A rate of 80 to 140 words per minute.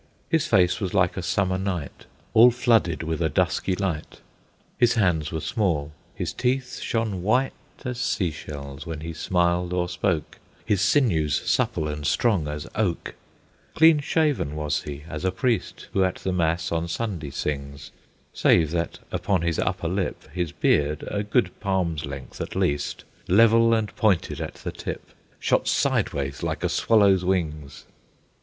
No: average, 160 wpm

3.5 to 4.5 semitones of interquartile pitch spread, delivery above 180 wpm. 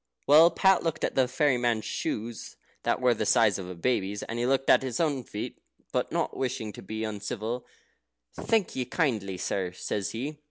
Yes: average, 4.2 semitones; average, 195 wpm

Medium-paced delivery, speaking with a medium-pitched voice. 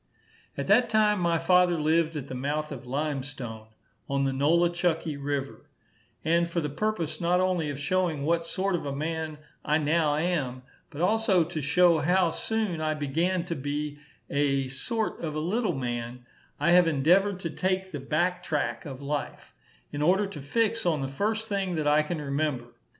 Yes: average, 185 wpm; medium, 155 Hz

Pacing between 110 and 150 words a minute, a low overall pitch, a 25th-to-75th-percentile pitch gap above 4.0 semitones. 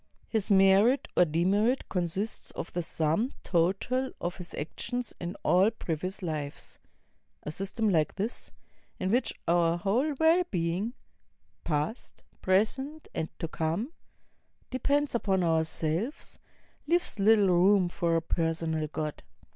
No: slow, 135 wpm; medium, 185 Hz; average, 5.3 semitones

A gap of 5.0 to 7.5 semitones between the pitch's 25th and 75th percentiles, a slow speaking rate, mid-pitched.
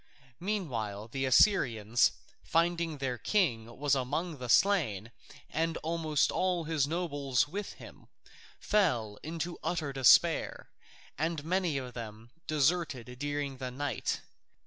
Yes: average, 5.3 semitones; slow, 125 wpm; medium, 145 Hz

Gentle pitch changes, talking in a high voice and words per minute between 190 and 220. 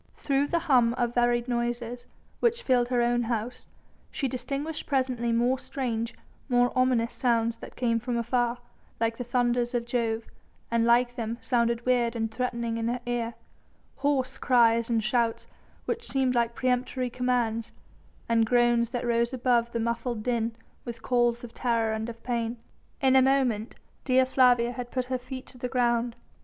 No: narrow, 1.4 semitones; high, 240 Hz; average, 170 wpm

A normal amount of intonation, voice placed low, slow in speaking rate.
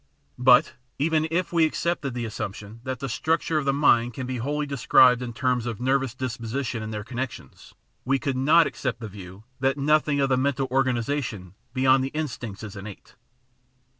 No: average, 3.3 semitones; low, 130 Hz; average, 190 wpm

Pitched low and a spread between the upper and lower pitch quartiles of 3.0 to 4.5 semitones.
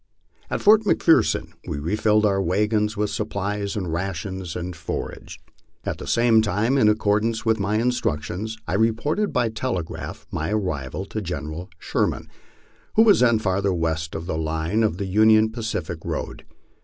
Yes: low, 105 Hz; average, 4.1 semitones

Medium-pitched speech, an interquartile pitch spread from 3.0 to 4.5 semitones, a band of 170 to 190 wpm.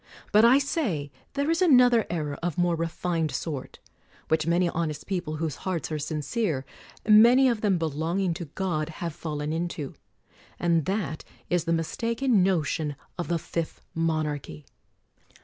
No: medium, 170 Hz; average, 4.1 semitones; average, 155 wpm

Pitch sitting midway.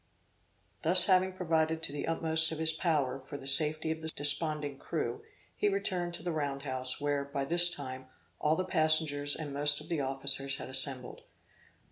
Yes: medium, 155 Hz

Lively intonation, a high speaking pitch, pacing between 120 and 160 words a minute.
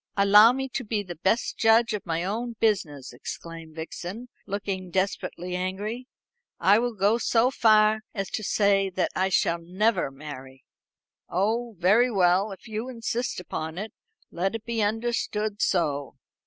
No: average, 3.9 semitones; high, 205 Hz; average, 155 wpm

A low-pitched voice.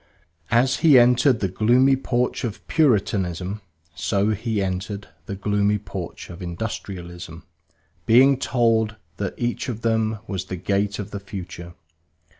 Yes: low, 105 Hz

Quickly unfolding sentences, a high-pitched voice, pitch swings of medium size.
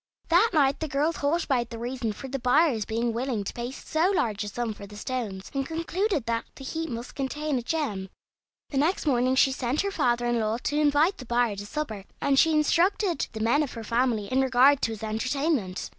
Yes: fast, 220 wpm; very high, 260 Hz; average, 4.7 semitones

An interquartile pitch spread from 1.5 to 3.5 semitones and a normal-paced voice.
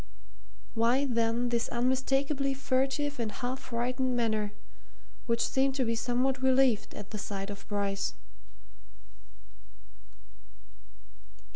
No: average, 2.7 semitones; slow, 105 wpm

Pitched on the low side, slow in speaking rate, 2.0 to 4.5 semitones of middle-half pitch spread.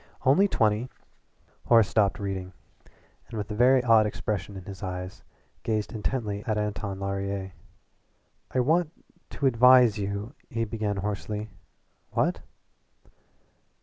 Yes: low, 105 Hz; slow, 130 wpm; average, 3.0 semitones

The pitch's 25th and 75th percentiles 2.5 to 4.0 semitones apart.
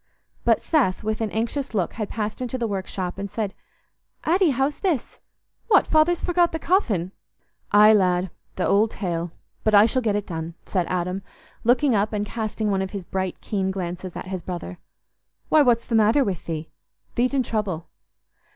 No: average, 4.7 semitones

